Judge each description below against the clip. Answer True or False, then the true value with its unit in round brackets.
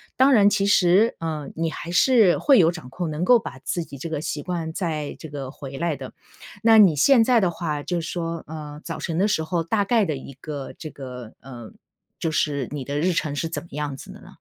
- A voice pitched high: False (160 Hz)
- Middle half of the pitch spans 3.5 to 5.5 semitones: True (4.0 semitones)